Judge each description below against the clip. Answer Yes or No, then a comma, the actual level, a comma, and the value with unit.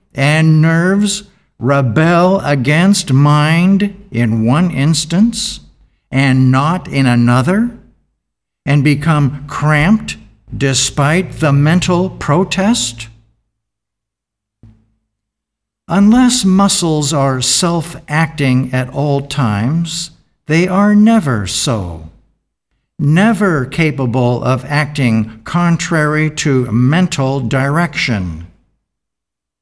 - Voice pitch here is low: No, medium, 145 Hz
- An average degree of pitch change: No, wide, 6.0 semitones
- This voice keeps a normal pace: No, slow, 80 wpm